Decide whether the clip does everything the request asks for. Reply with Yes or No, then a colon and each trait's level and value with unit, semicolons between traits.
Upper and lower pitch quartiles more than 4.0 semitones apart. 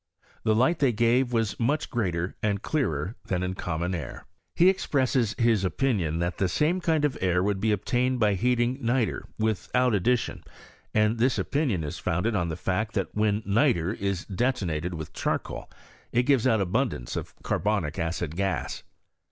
Yes: wide, 5.4 semitones